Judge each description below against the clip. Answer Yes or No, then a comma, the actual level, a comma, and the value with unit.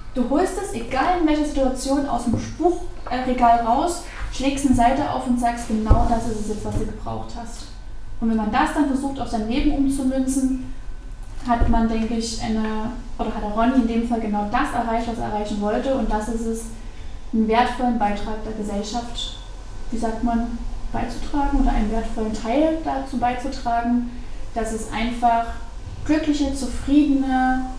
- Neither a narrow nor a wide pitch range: Yes, average, 3.0 semitones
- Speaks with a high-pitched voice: Yes, high, 235 Hz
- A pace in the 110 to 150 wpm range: No, average, 170 wpm